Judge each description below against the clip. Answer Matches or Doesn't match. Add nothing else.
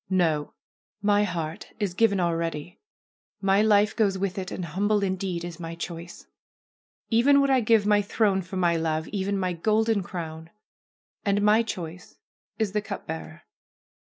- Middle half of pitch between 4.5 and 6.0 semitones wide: Doesn't match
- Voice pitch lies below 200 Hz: Matches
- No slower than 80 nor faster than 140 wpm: Doesn't match